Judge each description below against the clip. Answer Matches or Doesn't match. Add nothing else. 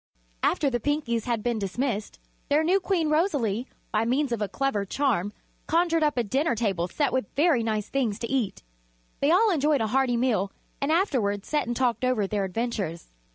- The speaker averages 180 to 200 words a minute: Matches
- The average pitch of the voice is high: Matches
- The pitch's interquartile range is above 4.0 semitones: Matches